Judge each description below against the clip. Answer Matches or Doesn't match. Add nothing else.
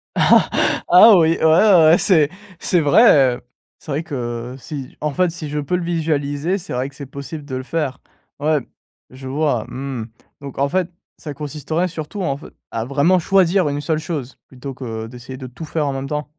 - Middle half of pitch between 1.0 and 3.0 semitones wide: Doesn't match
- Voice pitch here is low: Doesn't match